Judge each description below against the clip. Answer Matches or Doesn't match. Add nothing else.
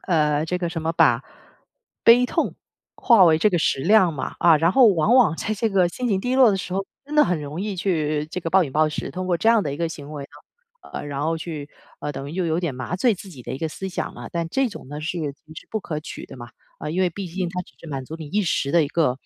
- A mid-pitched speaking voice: Matches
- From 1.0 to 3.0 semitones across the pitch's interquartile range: Doesn't match